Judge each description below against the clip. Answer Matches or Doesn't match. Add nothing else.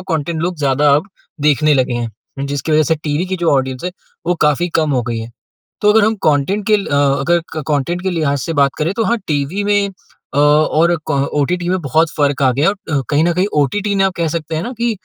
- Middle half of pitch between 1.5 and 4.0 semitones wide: Doesn't match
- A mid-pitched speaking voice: Matches